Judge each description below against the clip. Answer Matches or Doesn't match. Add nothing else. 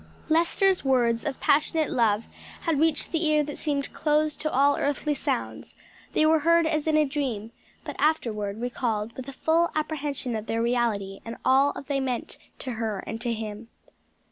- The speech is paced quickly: Doesn't match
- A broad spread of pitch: Doesn't match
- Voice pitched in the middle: Doesn't match